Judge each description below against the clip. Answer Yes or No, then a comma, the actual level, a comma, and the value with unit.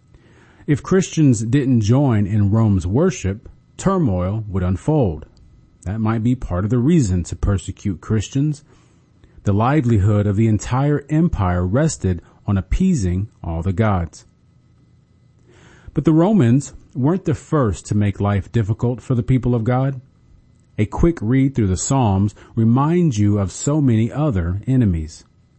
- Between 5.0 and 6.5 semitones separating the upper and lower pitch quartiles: Yes, wide, 5.6 semitones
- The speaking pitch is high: No, low, 115 Hz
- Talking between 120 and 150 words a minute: Yes, average, 140 wpm